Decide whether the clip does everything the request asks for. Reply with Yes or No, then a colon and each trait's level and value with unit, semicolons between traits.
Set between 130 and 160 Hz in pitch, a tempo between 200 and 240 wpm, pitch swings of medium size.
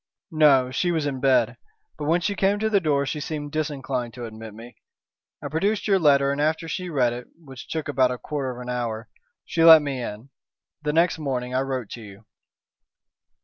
Yes: medium, 140 Hz; fast, 205 wpm; average, 4.2 semitones